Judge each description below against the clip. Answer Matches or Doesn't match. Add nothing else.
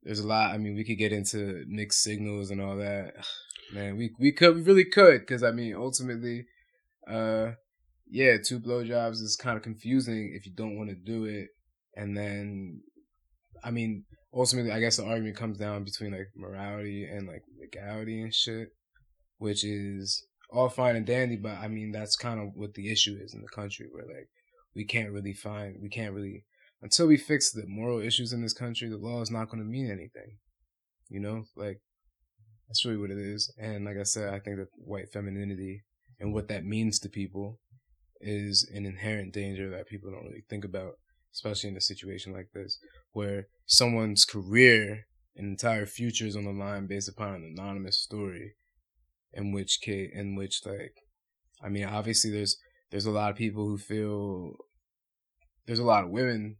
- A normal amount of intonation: Doesn't match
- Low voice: Matches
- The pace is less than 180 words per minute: Doesn't match